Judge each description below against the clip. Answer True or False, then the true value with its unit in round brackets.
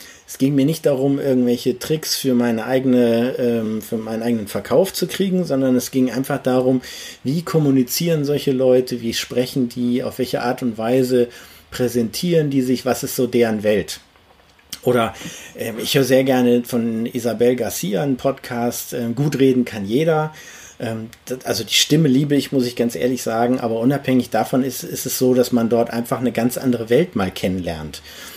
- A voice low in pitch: True (125 Hz)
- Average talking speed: True (175 wpm)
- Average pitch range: False (2.2 semitones)